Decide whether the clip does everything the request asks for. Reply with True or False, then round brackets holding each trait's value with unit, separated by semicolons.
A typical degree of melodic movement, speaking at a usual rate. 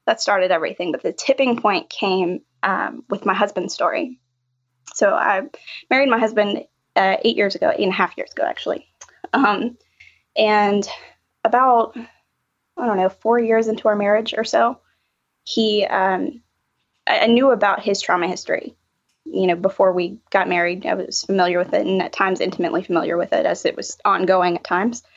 True (4.2 semitones; 180 wpm)